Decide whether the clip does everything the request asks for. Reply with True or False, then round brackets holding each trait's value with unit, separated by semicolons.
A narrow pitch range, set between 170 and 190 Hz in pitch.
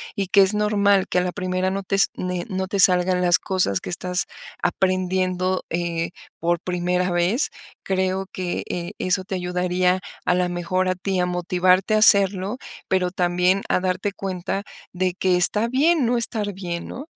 True (1.4 semitones; 185 Hz)